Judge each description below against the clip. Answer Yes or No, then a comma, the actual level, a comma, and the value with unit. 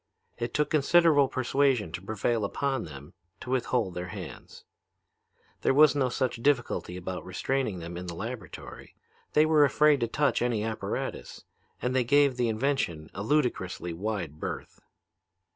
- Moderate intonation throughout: No, wide, 6.8 semitones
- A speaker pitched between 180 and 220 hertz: No, low, 120 Hz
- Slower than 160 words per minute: Yes, average, 150 wpm